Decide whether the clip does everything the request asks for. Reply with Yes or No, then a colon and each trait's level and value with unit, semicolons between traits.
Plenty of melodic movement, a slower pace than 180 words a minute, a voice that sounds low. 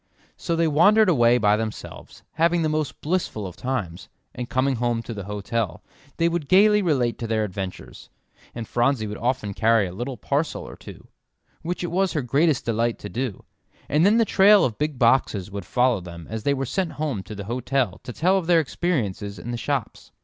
No: wide, 6.8 semitones; average, 200 wpm; low, 125 Hz